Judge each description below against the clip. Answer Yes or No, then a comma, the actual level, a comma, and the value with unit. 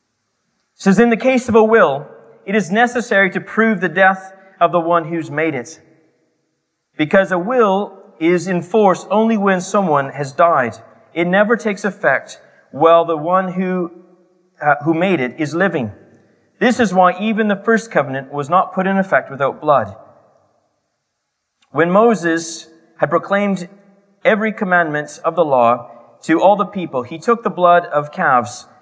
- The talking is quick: No, average, 160 wpm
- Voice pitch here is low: No, medium, 185 Hz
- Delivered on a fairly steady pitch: No, average, 3.7 semitones